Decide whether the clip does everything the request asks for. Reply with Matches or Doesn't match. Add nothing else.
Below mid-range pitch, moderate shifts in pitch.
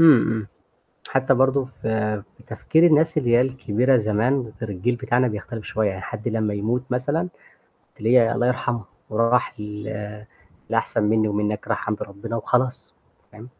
Matches